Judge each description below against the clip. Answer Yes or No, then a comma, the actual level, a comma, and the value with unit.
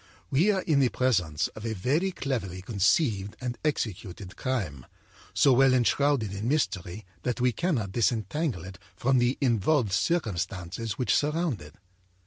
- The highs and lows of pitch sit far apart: Yes, wide, 6.2 semitones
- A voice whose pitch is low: Yes, low, 120 Hz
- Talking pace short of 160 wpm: Yes, average, 145 wpm